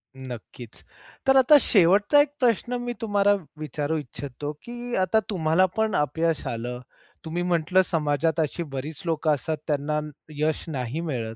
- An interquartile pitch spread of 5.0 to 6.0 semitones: Yes, wide, 5.4 semitones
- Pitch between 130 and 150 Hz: No, medium, 160 Hz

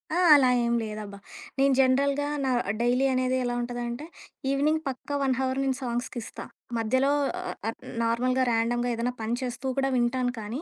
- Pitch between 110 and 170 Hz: No, very high, 250 Hz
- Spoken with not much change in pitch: Yes, narrow, 2.1 semitones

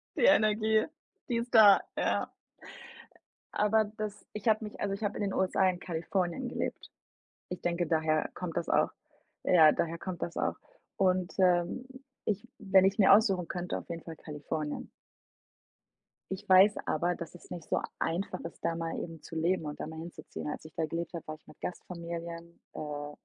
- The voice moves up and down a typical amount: Yes, average, 3.2 semitones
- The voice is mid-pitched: Yes, medium, 175 Hz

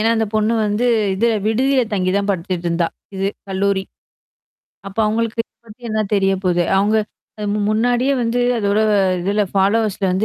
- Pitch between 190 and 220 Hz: Yes, high, 210 Hz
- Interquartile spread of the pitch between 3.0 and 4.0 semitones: No, narrow, 2.6 semitones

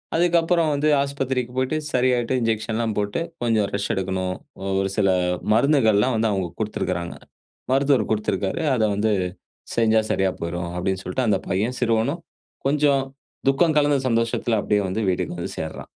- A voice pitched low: Yes, low, 115 Hz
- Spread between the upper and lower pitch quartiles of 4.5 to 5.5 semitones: Yes, average, 5.1 semitones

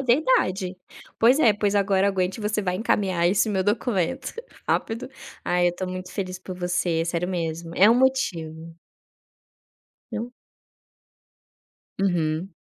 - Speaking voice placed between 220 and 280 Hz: No, high, 190 Hz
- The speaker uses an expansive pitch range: No, average, 3.1 semitones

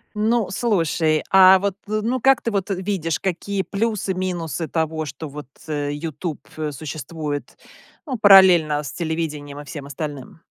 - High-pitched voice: No, medium, 165 Hz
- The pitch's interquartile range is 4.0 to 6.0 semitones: Yes, average, 4.6 semitones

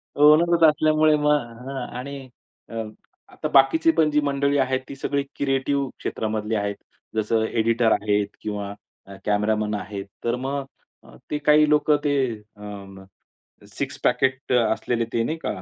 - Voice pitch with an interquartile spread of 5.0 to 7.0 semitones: Yes, average, 5.3 semitones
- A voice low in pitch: Yes, low, 130 Hz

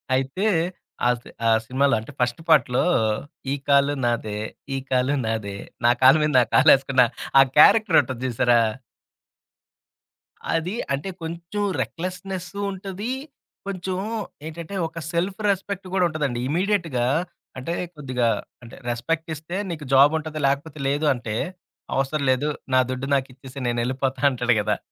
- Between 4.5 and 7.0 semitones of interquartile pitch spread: Yes, average, 5.0 semitones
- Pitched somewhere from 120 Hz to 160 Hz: Yes, medium, 140 Hz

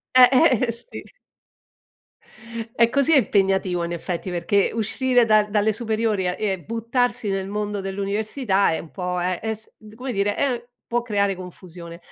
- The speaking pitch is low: No, high, 210 Hz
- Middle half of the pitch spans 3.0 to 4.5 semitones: Yes, average, 3.5 semitones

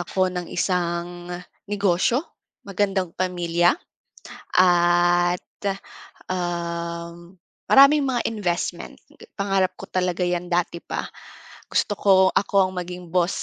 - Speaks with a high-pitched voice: No, medium, 180 Hz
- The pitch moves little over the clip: Yes, narrow, 1.8 semitones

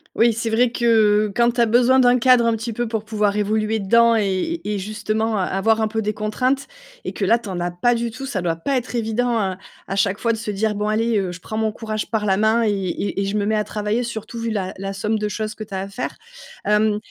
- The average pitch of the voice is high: Yes, high, 215 Hz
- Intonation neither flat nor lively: No, narrow, 2.1 semitones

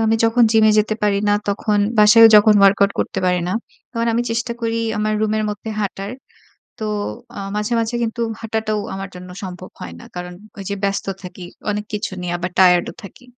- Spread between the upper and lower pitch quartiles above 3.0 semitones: No, narrow, 2.6 semitones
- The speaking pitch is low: No, high, 210 Hz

